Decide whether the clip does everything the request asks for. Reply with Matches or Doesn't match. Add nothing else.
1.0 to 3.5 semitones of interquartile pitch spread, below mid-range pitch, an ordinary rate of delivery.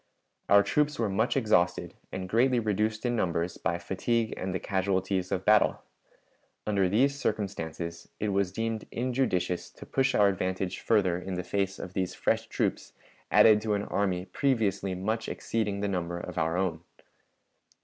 Matches